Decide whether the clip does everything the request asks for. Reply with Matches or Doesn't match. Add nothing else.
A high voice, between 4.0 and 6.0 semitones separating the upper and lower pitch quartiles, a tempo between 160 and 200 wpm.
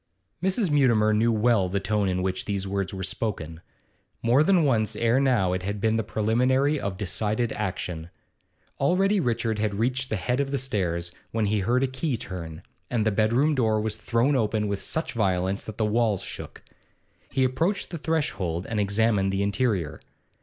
Doesn't match